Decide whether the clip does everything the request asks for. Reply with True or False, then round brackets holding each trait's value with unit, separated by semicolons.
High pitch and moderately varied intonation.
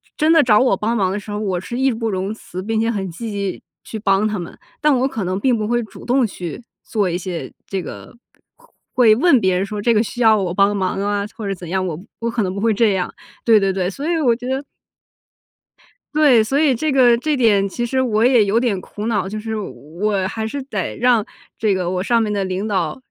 True (215 Hz; 3.7 semitones)